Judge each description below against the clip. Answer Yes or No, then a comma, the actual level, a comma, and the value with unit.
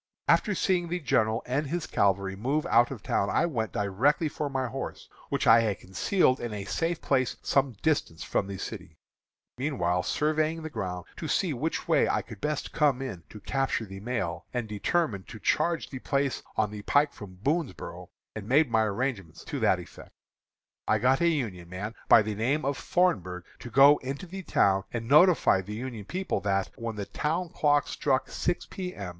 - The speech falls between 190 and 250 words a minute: Yes, average, 195 wpm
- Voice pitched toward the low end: Yes, low, 130 Hz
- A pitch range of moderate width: No, wide, 6.7 semitones